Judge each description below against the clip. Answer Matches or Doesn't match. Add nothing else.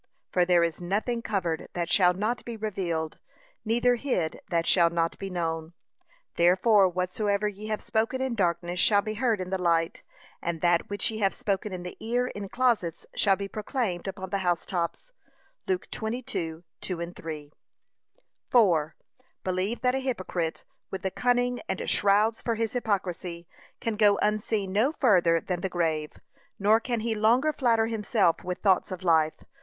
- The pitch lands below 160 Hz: Doesn't match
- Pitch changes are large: Doesn't match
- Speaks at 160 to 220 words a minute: Matches